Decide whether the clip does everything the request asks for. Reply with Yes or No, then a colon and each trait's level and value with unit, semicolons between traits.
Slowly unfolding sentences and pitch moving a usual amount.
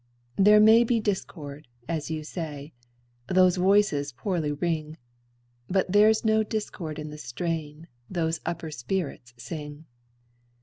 Yes: slow, 125 wpm; average, 4.7 semitones